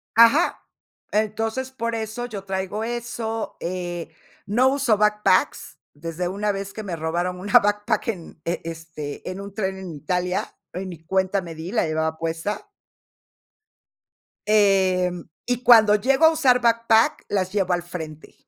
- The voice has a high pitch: Yes, high, 195 Hz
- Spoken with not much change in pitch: No, average, 4.1 semitones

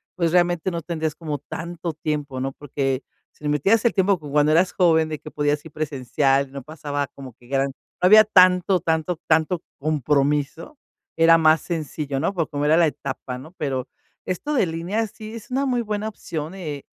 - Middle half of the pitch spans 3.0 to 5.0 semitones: Yes, average, 3.7 semitones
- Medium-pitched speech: Yes, medium, 155 Hz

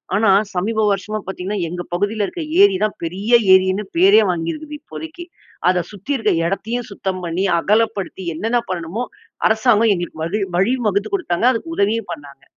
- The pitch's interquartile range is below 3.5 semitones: No, average, 3.9 semitones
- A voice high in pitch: Yes, high, 205 Hz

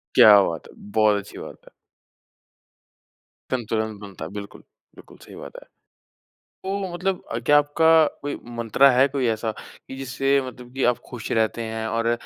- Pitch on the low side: Yes, low, 120 Hz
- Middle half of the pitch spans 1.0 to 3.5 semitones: No, average, 4.1 semitones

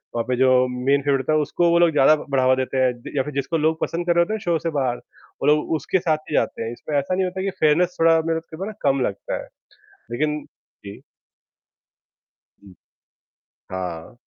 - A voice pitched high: No, medium, 150 Hz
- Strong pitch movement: No, average, 4.3 semitones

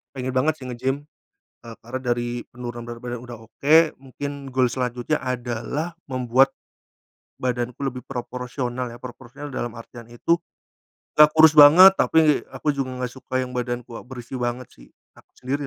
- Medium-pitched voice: No, low, 125 Hz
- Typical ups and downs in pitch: No, narrow, 2.1 semitones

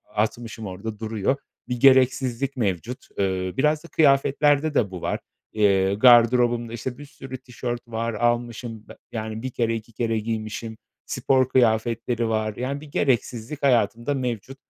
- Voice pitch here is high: No, low, 120 Hz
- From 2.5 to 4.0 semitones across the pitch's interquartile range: Yes, average, 2.9 semitones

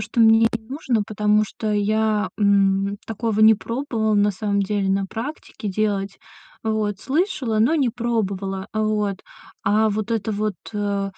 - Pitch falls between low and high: No, high, 215 Hz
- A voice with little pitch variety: Yes, narrow, 1.8 semitones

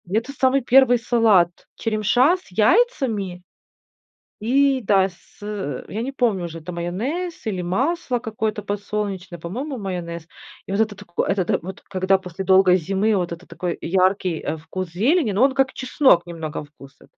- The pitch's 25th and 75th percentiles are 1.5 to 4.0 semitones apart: No, wide, 5.4 semitones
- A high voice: Yes, high, 200 Hz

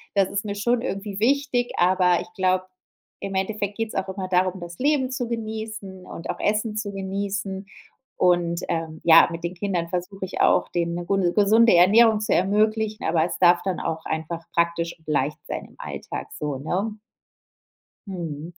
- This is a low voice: No, high, 190 Hz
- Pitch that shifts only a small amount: No, average, 3.6 semitones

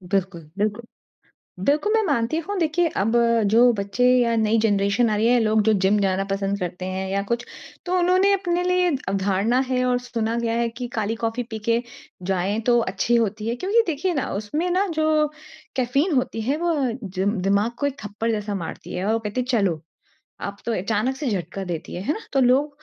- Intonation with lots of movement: Yes, wide, 5.8 semitones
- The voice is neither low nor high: No, high, 230 Hz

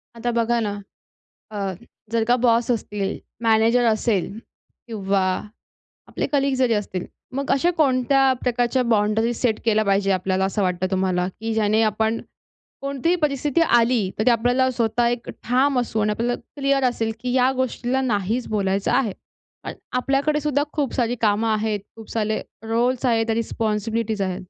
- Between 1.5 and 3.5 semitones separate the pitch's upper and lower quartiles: Yes, average, 3.1 semitones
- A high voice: Yes, high, 230 Hz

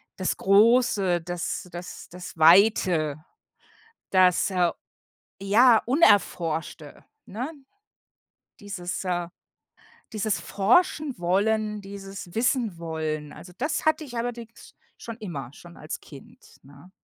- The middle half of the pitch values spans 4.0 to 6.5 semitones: Yes, average, 4.4 semitones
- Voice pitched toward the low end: No, high, 195 Hz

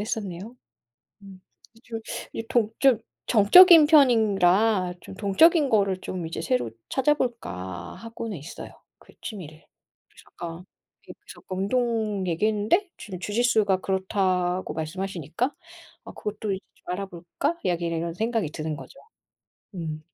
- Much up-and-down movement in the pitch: No, average, 4.4 semitones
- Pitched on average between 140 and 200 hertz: Yes, high, 195 Hz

